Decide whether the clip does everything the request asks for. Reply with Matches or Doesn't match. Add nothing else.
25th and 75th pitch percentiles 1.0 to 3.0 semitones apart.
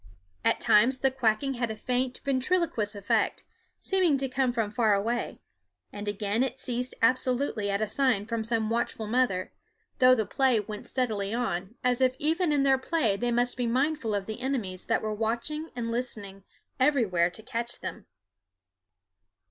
Doesn't match